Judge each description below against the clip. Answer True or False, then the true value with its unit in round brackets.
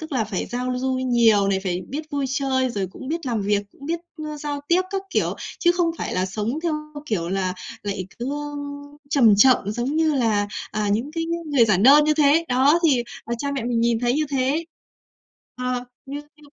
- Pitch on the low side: False (255 Hz)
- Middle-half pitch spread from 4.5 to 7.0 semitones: True (5.4 semitones)